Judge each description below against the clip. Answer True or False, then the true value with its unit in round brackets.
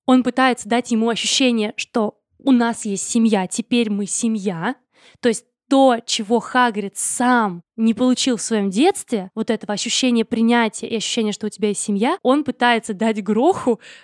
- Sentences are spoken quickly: True (165 wpm)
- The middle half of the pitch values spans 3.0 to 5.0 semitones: False (2.4 semitones)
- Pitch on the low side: False (230 Hz)